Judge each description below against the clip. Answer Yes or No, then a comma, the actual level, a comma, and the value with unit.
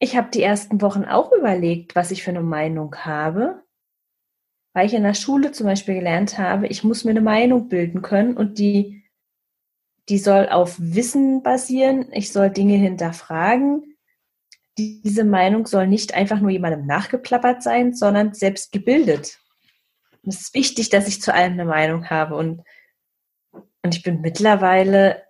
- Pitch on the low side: No, high, 200 Hz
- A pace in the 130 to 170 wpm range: Yes, average, 160 wpm